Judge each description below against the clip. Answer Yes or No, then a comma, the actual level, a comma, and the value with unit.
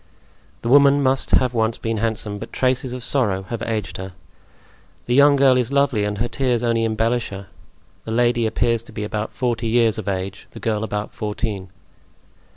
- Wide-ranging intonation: No, average, 3.0 semitones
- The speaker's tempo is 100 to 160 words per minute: No, average, 185 wpm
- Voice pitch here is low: Yes, low, 115 Hz